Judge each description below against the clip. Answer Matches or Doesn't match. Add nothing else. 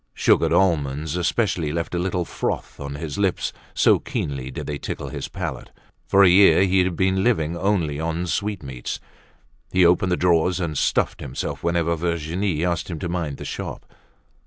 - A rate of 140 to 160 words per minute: Doesn't match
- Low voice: Matches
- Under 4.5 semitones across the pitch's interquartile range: Matches